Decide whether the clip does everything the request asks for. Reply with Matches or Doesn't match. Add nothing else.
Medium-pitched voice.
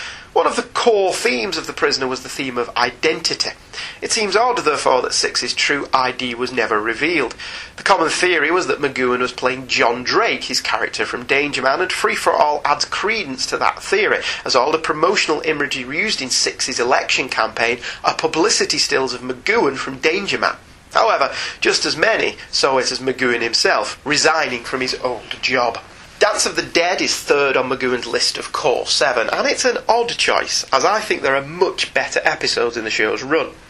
Doesn't match